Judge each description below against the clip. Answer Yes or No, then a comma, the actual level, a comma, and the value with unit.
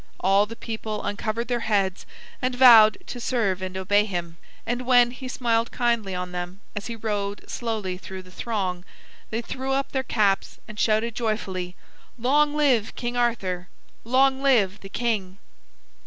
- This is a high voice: Yes, high, 220 Hz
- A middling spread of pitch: Yes, average, 3.9 semitones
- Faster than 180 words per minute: No, average, 160 wpm